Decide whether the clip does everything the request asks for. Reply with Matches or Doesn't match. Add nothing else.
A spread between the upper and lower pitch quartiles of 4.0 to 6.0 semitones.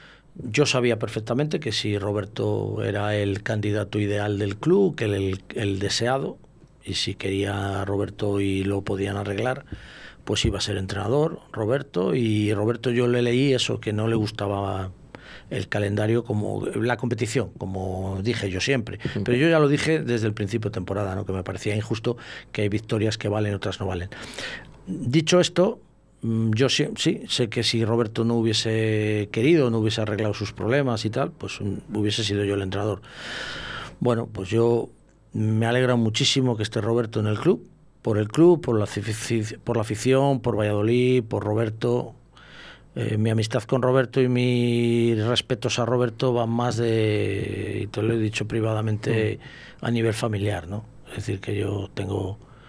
Doesn't match